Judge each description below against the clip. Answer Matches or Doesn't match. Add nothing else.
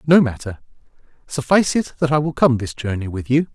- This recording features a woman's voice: Doesn't match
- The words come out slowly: Doesn't match